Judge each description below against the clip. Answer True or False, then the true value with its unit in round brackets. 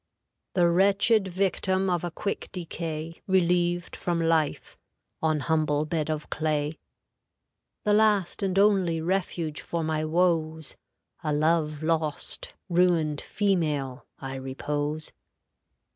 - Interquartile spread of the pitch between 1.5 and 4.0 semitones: True (2.9 semitones)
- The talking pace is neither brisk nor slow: False (115 wpm)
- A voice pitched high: False (165 Hz)